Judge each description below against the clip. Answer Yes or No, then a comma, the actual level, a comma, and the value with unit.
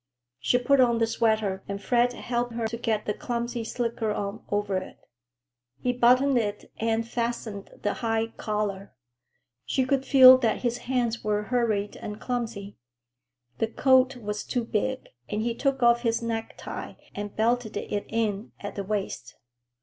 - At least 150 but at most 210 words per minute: Yes, average, 160 wpm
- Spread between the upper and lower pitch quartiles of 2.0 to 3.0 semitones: Yes, average, 2.7 semitones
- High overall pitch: Yes, high, 230 Hz